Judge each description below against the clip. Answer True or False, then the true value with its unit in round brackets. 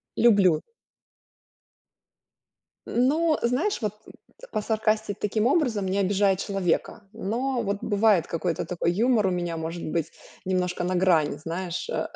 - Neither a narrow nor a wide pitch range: True (4.1 semitones)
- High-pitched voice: True (200 Hz)